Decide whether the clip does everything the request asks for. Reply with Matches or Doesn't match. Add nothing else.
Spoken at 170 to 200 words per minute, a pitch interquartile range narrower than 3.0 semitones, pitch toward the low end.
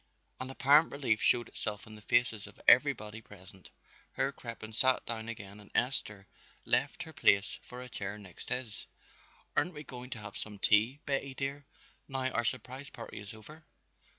Doesn't match